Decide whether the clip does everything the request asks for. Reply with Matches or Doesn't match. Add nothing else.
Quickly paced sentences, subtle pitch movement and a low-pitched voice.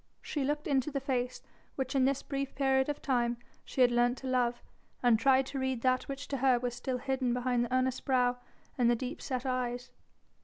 Doesn't match